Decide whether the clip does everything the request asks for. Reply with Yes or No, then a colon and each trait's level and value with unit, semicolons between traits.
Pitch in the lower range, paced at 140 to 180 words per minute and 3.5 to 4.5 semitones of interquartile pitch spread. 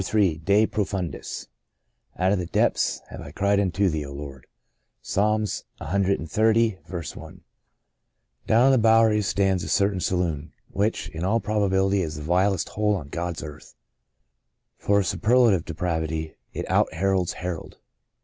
Yes: very low, 95 Hz; average, 150 wpm; average, 4.1 semitones